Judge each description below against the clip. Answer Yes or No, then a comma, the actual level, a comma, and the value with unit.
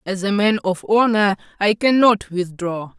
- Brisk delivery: No, average, 160 wpm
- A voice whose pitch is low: No, high, 200 Hz